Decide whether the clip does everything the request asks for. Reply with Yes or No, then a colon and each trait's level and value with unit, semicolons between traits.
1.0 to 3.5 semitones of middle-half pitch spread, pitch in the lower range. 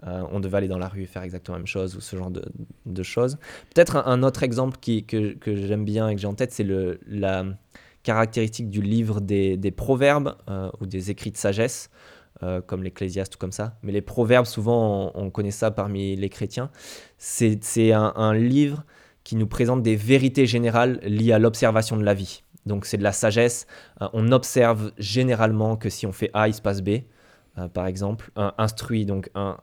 Yes: average, 3.1 semitones; low, 105 Hz